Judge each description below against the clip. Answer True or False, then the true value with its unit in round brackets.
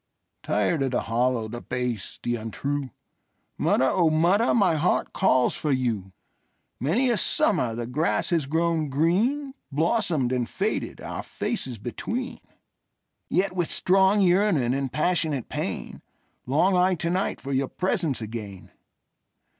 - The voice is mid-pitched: True (155 Hz)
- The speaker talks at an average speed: False (120 wpm)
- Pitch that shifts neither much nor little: False (6.8 semitones)